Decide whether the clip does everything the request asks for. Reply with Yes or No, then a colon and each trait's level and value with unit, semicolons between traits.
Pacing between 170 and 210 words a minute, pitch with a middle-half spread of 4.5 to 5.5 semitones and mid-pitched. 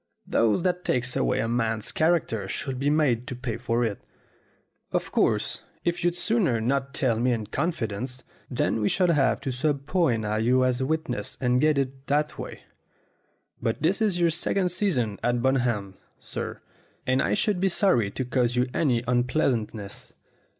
No: average, 175 wpm; average, 5.1 semitones; low, 130 Hz